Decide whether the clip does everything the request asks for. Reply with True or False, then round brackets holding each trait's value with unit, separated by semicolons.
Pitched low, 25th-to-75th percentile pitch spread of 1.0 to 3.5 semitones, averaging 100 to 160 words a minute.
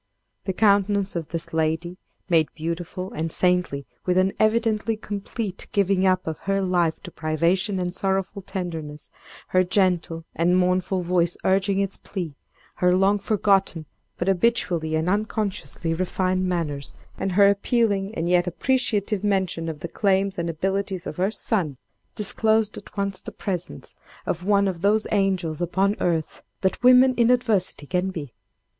False (185 Hz; 2.8 semitones; 150 wpm)